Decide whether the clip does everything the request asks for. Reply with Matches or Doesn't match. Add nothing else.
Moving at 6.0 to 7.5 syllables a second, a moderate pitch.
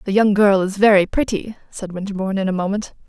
Doesn't match